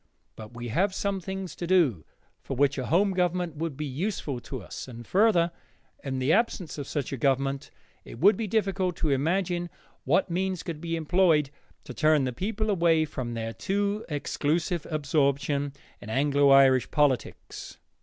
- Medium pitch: Yes, medium, 155 Hz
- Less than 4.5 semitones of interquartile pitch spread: No, average, 5.1 semitones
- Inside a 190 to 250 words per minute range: No, average, 170 wpm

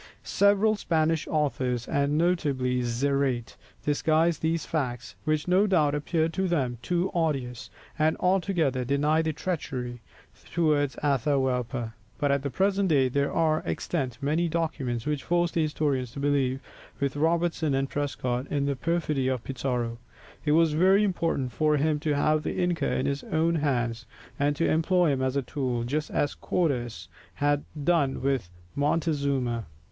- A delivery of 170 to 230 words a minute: No, average, 155 wpm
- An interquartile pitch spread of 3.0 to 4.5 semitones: Yes, average, 3.7 semitones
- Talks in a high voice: No, medium, 145 Hz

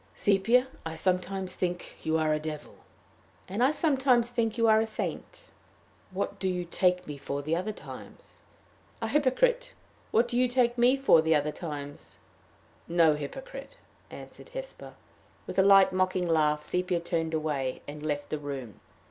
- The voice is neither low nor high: Yes, medium, 180 Hz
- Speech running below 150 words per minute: No, average, 165 wpm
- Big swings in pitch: Yes, wide, 7.4 semitones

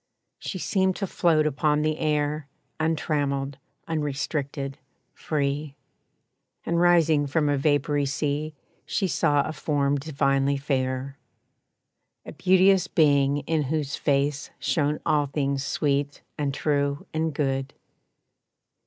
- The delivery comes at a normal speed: No, slow, 115 wpm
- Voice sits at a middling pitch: Yes, medium, 145 Hz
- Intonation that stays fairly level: Yes, narrow, 1.9 semitones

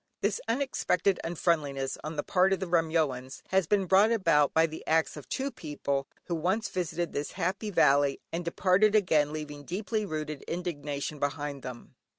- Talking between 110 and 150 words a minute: No, average, 165 wpm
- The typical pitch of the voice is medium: Yes, medium, 165 Hz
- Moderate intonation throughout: Yes, average, 4.3 semitones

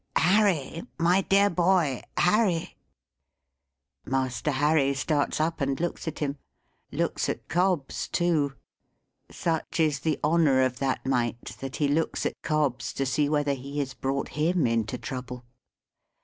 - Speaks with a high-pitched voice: No, medium, 145 Hz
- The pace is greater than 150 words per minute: No, average, 140 wpm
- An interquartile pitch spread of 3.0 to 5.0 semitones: Yes, average, 3.8 semitones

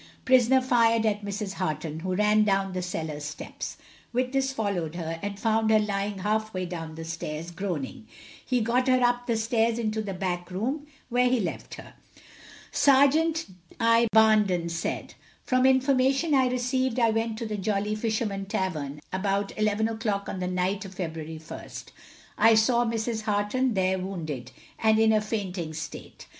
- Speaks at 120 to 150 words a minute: No, average, 165 wpm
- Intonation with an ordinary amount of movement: Yes, average, 4.1 semitones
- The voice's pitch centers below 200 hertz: No, high, 210 Hz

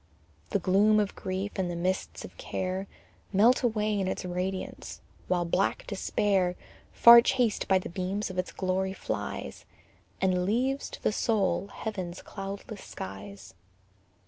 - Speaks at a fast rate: No, average, 145 wpm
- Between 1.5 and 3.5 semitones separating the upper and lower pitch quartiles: Yes, narrow, 2.4 semitones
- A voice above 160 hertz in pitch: Yes, high, 190 Hz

